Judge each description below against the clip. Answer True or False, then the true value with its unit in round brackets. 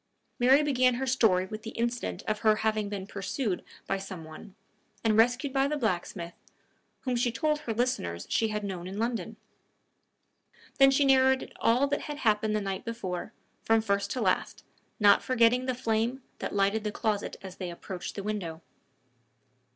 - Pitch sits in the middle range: False (220 Hz)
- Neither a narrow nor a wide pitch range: True (4.2 semitones)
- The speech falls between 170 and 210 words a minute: True (175 wpm)